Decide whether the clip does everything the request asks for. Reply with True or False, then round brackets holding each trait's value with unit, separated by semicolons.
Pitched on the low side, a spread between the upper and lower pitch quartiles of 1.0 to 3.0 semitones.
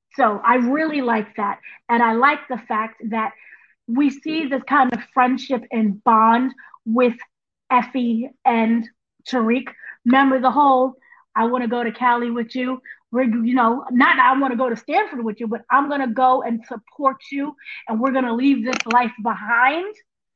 False (250 Hz; 2.5 semitones)